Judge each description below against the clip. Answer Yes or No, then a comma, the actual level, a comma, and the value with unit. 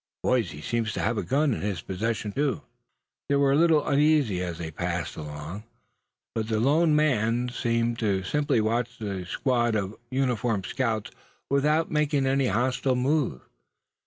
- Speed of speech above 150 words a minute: Yes, average, 160 wpm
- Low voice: Yes, low, 120 Hz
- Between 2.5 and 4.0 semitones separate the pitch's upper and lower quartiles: No, average, 5.0 semitones